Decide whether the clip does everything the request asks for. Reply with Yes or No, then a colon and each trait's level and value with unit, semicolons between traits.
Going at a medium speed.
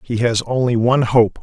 No: fast, 210 wpm